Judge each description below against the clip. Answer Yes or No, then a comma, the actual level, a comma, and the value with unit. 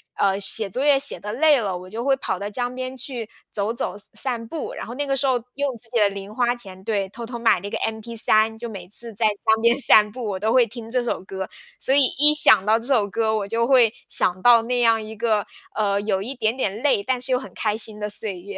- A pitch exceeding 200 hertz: Yes, high, 225 Hz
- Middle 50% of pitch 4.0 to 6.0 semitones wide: No, average, 3.3 semitones